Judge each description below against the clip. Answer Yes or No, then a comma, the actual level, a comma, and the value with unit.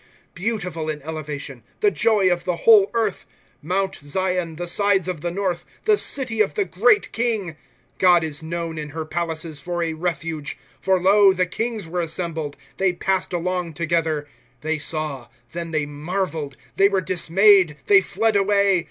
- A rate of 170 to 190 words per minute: Yes, average, 180 wpm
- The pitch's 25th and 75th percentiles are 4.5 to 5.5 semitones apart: No, average, 3.6 semitones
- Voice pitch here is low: No, medium, 175 Hz